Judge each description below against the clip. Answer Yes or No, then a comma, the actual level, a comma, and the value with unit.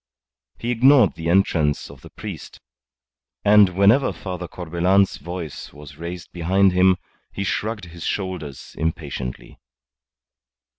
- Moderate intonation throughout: Yes, average, 3.1 semitones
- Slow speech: Yes, slow, 115 wpm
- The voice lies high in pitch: No, very low, 90 Hz